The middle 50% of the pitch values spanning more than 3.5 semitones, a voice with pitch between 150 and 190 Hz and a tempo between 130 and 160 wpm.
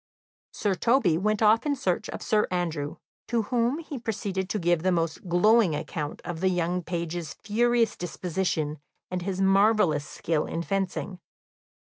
Yes: average, 4.1 semitones; medium, 185 Hz; average, 155 wpm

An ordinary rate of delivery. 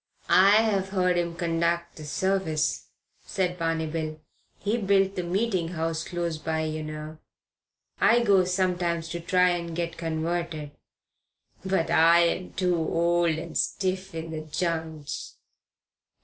No: slow, 130 wpm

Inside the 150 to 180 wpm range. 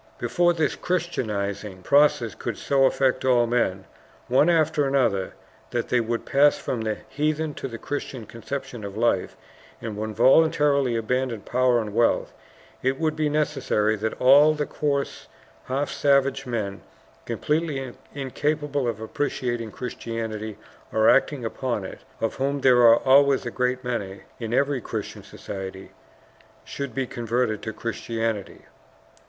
No: average, 140 wpm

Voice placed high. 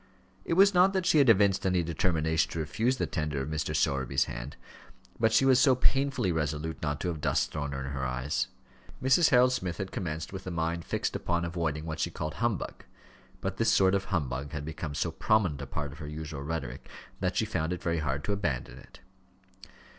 No: very low, 80 Hz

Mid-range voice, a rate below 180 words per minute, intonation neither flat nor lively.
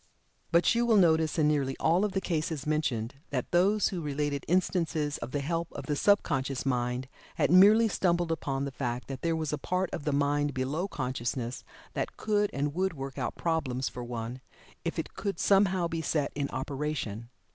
No: medium, 150 Hz; average, 190 wpm; average, 4.5 semitones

